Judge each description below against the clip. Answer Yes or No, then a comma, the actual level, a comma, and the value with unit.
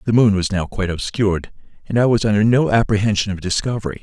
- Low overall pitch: Yes, low, 105 Hz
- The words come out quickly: Yes, fast, 210 wpm